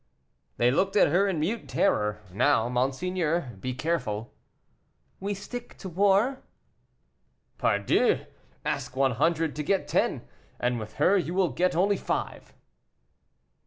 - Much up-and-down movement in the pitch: Yes, wide, 7.5 semitones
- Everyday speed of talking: No, slow, 130 wpm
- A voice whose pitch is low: No, medium, 160 Hz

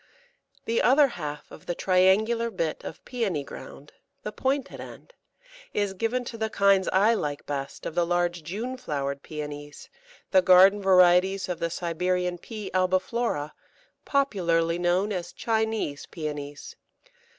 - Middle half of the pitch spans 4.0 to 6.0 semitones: Yes, average, 4.7 semitones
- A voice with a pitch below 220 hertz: Yes, medium, 185 Hz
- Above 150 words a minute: No, average, 140 wpm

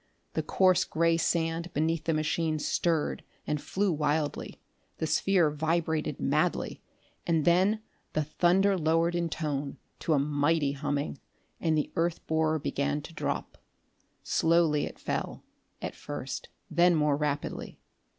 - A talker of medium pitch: Yes, medium, 160 Hz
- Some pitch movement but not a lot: No, narrow, 2.2 semitones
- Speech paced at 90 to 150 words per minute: Yes, slow, 135 wpm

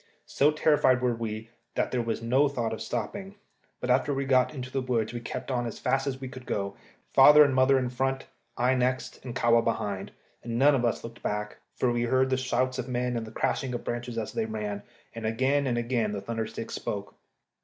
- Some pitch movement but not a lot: No, narrow, 2.3 semitones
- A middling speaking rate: No, fast, 230 wpm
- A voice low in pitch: Yes, low, 125 Hz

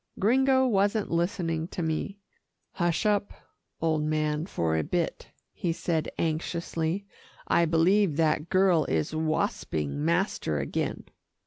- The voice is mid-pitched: Yes, medium, 165 Hz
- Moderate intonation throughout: Yes, average, 3.8 semitones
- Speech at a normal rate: No, slow, 120 wpm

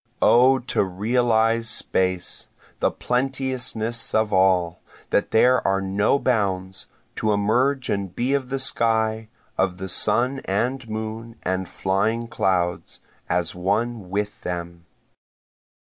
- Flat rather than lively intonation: No, average, 4.2 semitones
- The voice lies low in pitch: Yes, low, 110 Hz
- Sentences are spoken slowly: Yes, slow, 120 wpm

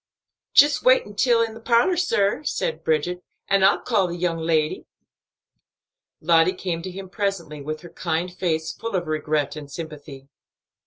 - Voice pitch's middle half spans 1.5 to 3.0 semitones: No, average, 4.1 semitones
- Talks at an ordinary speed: Yes, average, 155 wpm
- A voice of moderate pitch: Yes, medium, 175 Hz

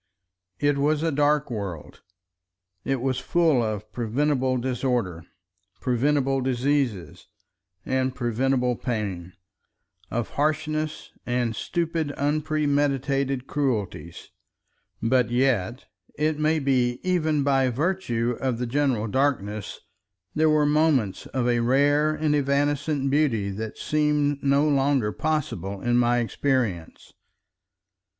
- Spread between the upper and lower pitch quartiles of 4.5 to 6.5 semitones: No, average, 3.7 semitones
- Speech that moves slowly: Yes, slow, 110 wpm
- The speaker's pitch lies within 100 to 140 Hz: Yes, low, 135 Hz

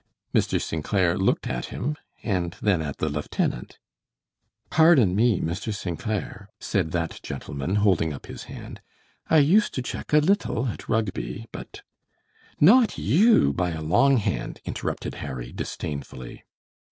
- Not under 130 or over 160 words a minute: Yes, average, 150 wpm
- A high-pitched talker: No, very low, 95 Hz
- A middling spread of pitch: No, wide, 8.6 semitones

